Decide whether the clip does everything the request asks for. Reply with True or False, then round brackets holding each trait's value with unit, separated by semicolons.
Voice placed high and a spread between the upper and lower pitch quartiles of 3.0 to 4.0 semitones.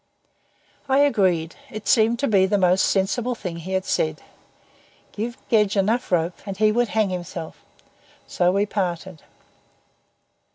True (195 Hz; 3.4 semitones)